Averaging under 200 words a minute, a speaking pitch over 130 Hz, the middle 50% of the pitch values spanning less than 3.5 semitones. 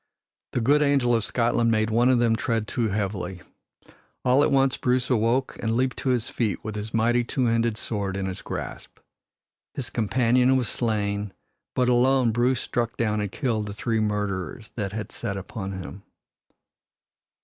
No: average, 170 wpm; low, 115 Hz; average, 3.0 semitones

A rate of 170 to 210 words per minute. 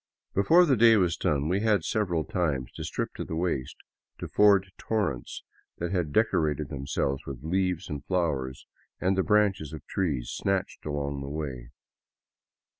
No: average, 160 wpm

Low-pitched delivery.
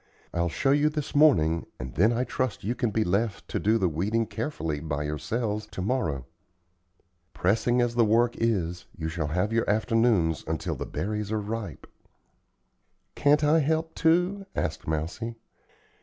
Yes: low, 110 Hz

